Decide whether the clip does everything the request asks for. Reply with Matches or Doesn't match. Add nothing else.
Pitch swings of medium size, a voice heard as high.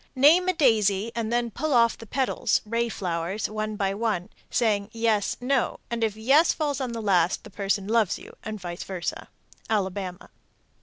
Matches